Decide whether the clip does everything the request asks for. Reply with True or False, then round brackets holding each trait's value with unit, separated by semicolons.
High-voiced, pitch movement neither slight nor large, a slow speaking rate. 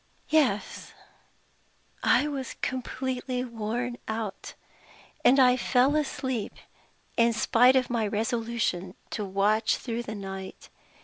True (235 Hz; 3.1 semitones; 110 wpm)